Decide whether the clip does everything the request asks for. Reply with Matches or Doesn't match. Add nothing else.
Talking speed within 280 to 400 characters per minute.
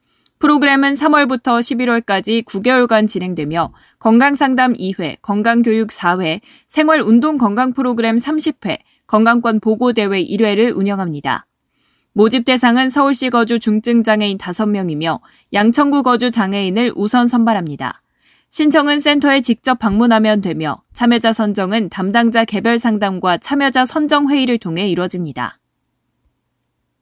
Matches